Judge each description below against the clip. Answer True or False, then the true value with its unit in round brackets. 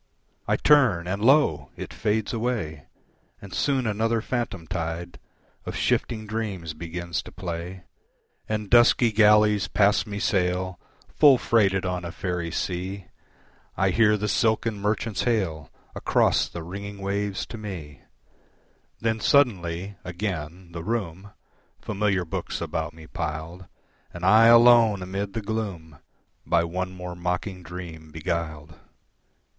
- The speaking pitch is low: True (95 Hz)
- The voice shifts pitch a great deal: False (3.9 semitones)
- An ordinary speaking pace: False (130 wpm)